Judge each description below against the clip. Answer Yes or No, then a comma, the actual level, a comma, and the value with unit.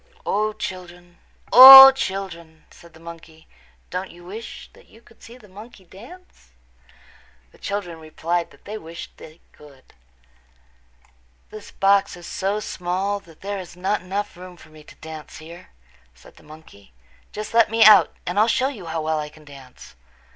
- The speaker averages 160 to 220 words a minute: Yes, average, 170 wpm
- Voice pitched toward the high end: No, medium, 180 Hz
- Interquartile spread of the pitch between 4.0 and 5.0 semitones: Yes, average, 4.4 semitones